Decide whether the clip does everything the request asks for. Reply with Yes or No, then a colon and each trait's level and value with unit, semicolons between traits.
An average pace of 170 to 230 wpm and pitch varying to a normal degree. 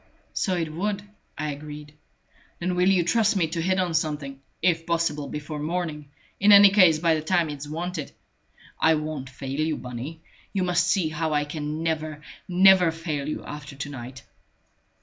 Yes: average, 175 wpm; average, 3.1 semitones